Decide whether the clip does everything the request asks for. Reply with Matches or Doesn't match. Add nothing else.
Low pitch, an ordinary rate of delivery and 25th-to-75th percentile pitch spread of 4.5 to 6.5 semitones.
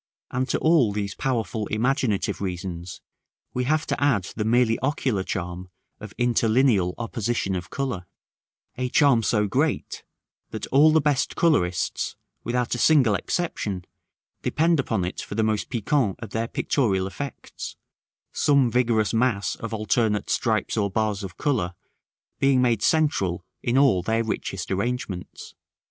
Matches